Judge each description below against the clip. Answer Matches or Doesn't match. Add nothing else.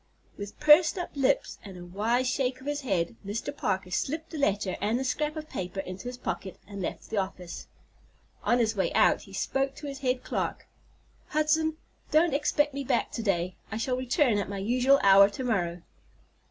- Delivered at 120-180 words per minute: Doesn't match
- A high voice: Matches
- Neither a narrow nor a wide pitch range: Doesn't match